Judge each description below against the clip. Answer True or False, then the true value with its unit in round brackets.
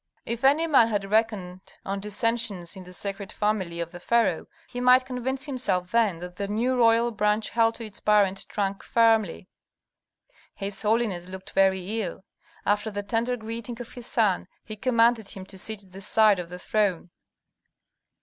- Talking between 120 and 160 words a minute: False (175 wpm)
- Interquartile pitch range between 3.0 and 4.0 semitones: True (3.3 semitones)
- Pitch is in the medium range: False (210 Hz)